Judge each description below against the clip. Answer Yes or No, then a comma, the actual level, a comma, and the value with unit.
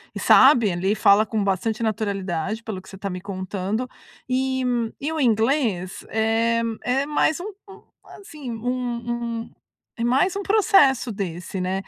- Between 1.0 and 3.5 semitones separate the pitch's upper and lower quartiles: No, average, 4.7 semitones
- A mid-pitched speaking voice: No, high, 225 Hz